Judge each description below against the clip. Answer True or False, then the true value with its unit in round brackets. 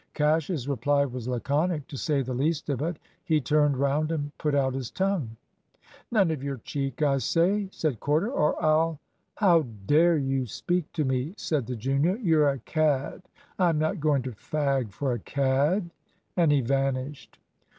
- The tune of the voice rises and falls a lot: False (3.2 semitones)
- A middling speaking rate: True (175 wpm)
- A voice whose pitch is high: False (145 Hz)